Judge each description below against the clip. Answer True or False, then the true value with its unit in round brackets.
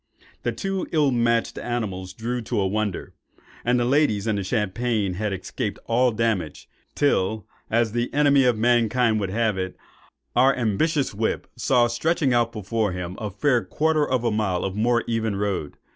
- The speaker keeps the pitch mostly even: False (3.2 semitones)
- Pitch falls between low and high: False (115 Hz)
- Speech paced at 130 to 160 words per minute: False (175 wpm)